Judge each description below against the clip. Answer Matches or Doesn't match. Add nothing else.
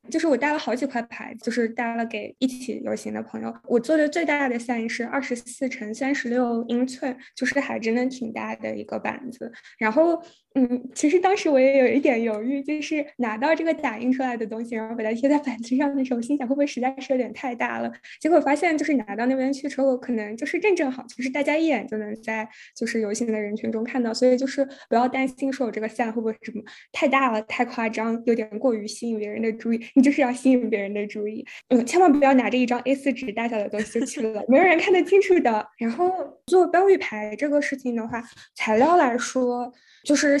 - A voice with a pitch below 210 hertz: Doesn't match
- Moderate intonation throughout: Matches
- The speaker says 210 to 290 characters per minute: Doesn't match